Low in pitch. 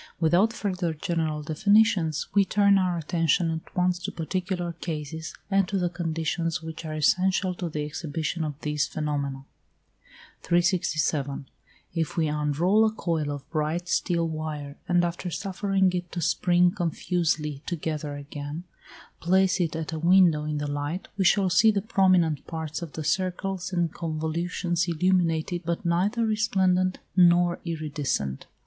No: medium, 170 Hz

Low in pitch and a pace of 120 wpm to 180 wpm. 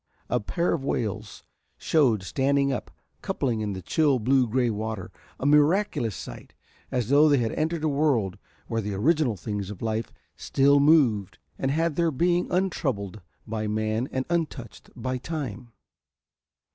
Yes: low, 125 Hz; average, 155 wpm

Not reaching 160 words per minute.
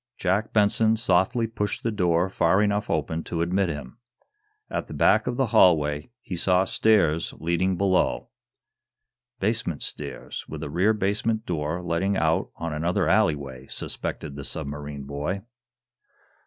Yes: average, 140 wpm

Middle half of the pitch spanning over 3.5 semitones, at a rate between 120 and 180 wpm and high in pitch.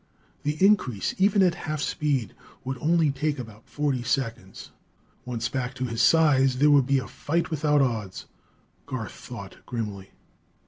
No: average, 4.2 semitones; average, 150 wpm; low, 135 Hz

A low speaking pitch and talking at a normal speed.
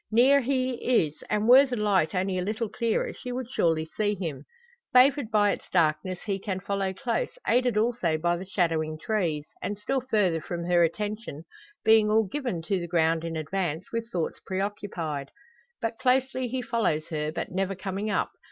No: high, 200 Hz; average, 180 wpm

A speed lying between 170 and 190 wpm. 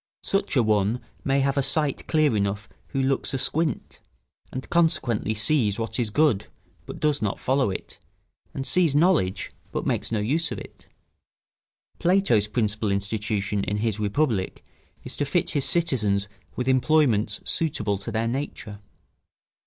No: average, 150 wpm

